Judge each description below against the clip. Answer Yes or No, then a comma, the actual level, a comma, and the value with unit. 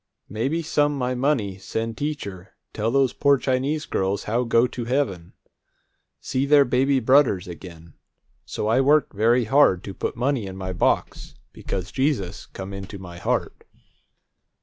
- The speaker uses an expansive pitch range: Yes, wide, 6.1 semitones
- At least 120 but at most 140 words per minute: No, average, 150 wpm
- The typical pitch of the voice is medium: No, low, 115 Hz